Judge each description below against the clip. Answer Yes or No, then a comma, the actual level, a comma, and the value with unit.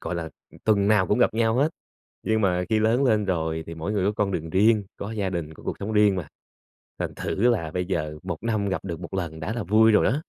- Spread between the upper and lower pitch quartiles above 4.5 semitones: No, average, 4.2 semitones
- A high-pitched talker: No, low, 100 Hz